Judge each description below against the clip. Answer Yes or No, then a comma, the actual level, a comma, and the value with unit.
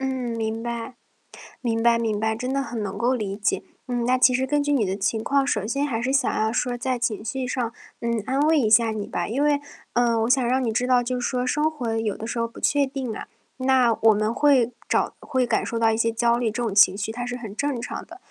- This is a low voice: No, high, 240 Hz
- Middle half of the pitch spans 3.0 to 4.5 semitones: No, narrow, 2.6 semitones